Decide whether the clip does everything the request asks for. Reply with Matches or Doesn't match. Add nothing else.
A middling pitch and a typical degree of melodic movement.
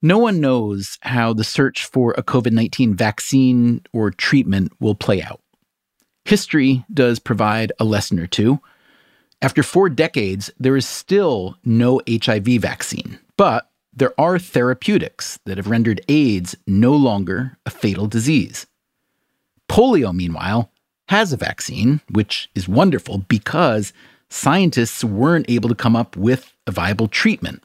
Doesn't match